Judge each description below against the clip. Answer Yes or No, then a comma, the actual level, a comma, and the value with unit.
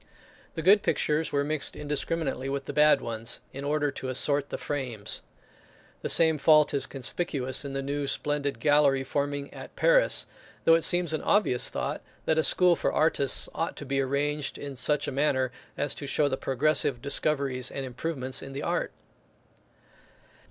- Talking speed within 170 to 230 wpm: Yes, average, 175 wpm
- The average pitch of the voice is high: No, medium, 145 Hz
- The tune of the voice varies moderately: No, narrow, 2.1 semitones